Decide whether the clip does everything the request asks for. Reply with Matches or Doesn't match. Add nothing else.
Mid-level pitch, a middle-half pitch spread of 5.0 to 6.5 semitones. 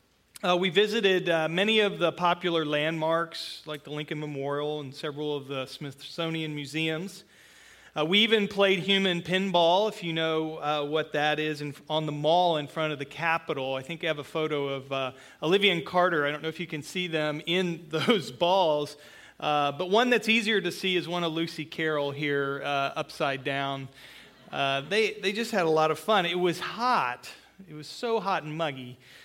Doesn't match